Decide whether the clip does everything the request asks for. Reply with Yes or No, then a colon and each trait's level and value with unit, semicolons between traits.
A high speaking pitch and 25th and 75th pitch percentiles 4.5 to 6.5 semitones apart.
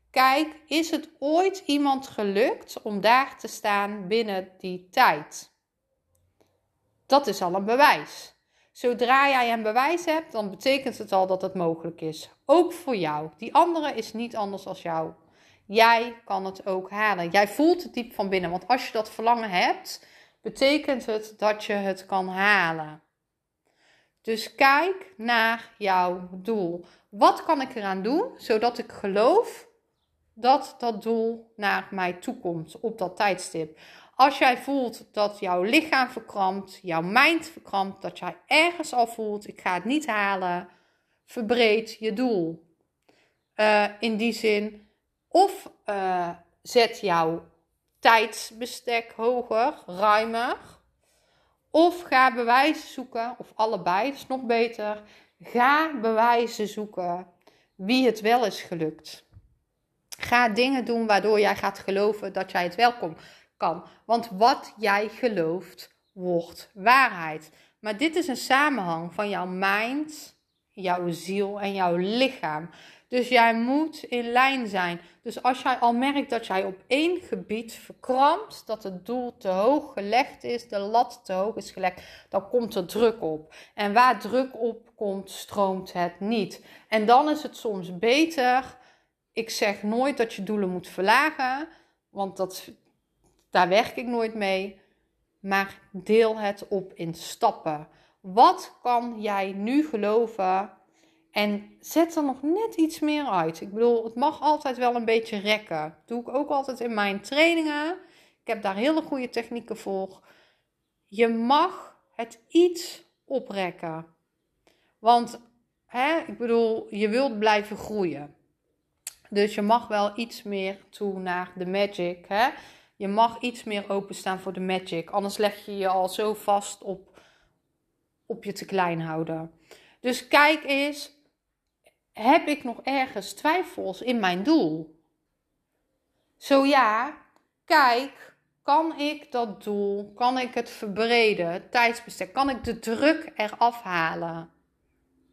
Yes: high, 220 Hz; average, 4.8 semitones